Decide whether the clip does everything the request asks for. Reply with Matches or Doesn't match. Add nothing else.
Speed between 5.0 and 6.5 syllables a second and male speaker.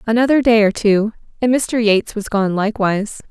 Doesn't match